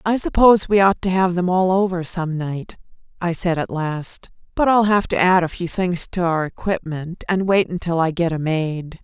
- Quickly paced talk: Yes, fast, 220 wpm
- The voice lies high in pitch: No, medium, 175 Hz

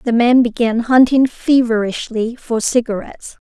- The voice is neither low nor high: No, high, 235 Hz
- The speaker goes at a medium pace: No, slow, 120 wpm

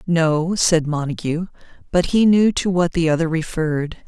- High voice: No, medium, 165 Hz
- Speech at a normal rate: Yes, average, 160 wpm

